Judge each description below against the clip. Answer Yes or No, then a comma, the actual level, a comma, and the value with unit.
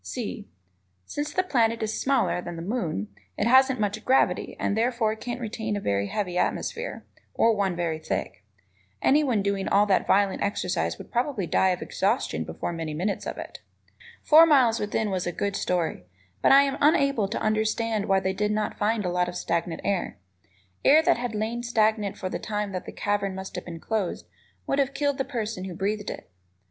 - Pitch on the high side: Yes, high, 210 Hz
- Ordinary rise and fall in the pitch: Yes, average, 4.2 semitones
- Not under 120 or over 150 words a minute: No, average, 195 wpm